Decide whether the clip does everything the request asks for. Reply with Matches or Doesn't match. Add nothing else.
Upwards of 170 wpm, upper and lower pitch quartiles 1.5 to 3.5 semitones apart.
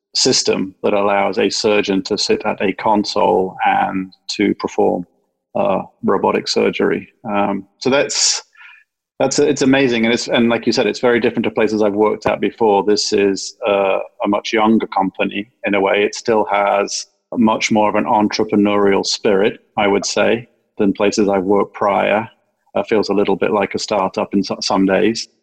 Matches